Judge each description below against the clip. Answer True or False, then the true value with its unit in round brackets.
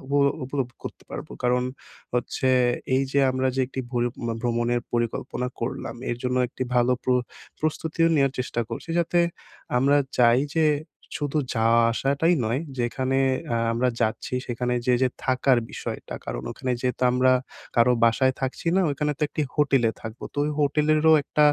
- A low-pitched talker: True (130 Hz)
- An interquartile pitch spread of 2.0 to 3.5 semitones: True (2.7 semitones)